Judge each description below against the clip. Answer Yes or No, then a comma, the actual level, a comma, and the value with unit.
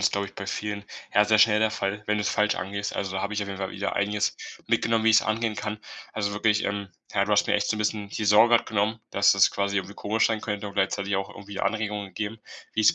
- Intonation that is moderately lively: No, narrow, 1.2 semitones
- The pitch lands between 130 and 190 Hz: No, low, 105 Hz